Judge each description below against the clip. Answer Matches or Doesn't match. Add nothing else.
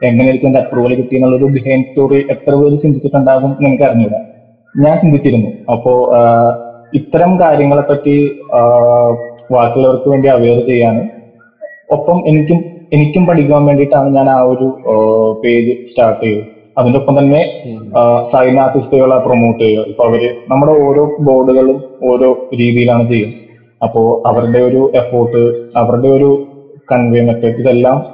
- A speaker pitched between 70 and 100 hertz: Doesn't match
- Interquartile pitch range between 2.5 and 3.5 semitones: Matches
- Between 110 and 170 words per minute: Matches